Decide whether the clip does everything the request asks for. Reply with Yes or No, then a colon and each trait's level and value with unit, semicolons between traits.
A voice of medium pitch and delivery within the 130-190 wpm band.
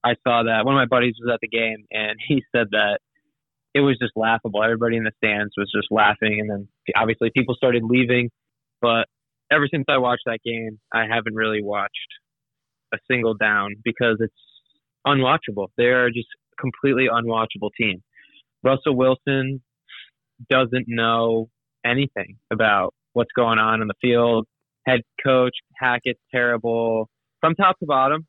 No: low, 120 Hz; average, 160 wpm